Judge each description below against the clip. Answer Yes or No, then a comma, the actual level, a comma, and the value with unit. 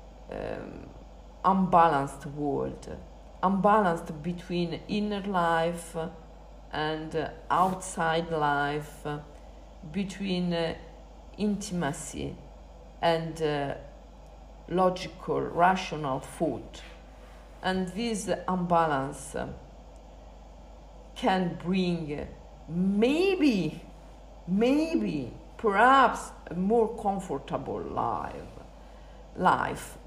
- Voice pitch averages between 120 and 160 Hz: No, medium, 170 Hz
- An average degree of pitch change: Yes, average, 4.1 semitones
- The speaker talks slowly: Yes, slow, 70 wpm